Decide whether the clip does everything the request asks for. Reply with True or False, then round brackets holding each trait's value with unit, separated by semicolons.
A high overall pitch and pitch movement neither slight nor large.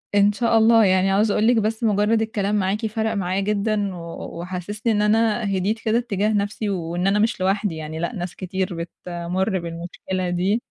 True (200 Hz; 3.0 semitones)